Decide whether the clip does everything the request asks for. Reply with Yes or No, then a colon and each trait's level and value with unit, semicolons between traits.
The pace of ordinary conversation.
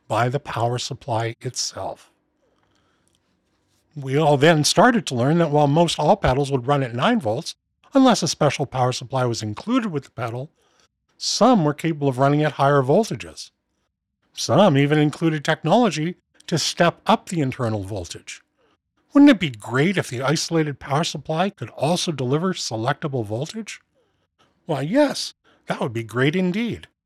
Yes: average, 155 wpm